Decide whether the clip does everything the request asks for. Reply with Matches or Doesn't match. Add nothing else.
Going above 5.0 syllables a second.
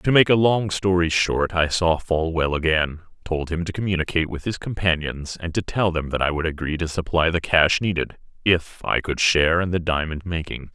Matches